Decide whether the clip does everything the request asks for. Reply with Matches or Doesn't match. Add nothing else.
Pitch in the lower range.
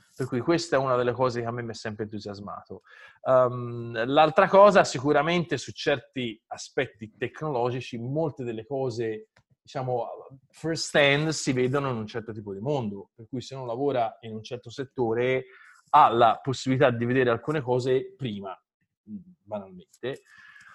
Matches